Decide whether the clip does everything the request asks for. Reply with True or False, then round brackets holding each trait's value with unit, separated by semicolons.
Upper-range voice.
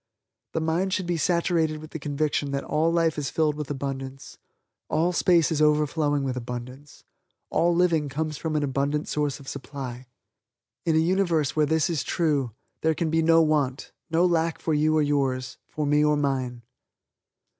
False (150 Hz)